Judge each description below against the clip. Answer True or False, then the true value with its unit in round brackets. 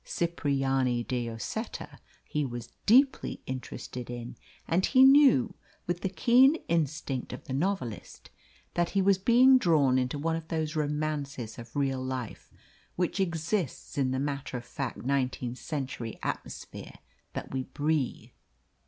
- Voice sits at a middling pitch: True (145 Hz)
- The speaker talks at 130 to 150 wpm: True (140 wpm)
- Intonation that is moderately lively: True (4.9 semitones)